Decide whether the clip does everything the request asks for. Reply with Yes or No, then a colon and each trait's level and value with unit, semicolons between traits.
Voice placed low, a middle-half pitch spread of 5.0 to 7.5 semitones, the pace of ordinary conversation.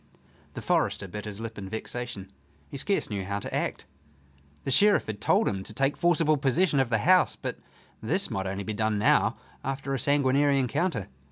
Yes: low, 125 Hz; wide, 5.6 semitones; average, 190 wpm